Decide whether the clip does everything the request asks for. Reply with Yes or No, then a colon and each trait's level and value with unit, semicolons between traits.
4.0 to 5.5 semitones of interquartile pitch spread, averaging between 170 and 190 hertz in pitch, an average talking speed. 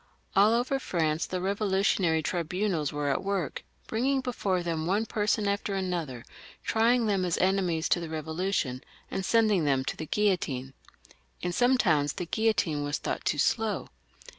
Yes: average, 4.9 semitones; medium, 185 Hz; average, 165 wpm